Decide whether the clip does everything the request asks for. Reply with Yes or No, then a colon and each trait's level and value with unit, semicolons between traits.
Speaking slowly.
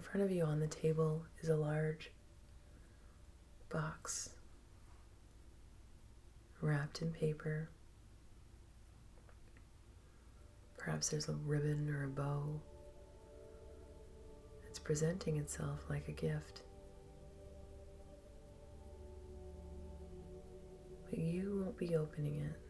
Yes: slow, 85 wpm